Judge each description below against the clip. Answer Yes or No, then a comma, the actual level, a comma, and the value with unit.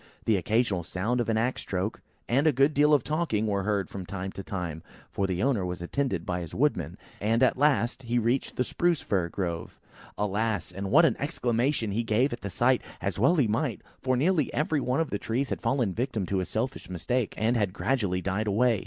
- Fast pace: Yes, fast, 225 wpm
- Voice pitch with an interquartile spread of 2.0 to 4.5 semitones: No, average, 5.1 semitones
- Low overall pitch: Yes, low, 115 Hz